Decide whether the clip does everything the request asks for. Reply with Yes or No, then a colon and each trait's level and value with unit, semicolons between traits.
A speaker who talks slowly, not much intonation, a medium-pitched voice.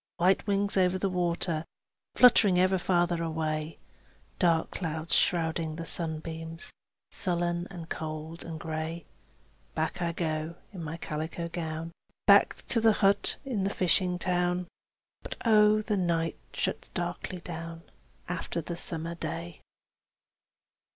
Yes: slow, 130 wpm; narrow, 2.0 semitones; medium, 170 Hz